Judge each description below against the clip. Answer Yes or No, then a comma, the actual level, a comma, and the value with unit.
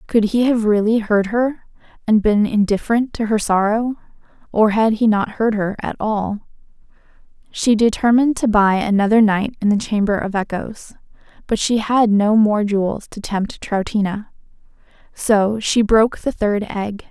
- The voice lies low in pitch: No, high, 215 Hz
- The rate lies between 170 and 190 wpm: No, average, 160 wpm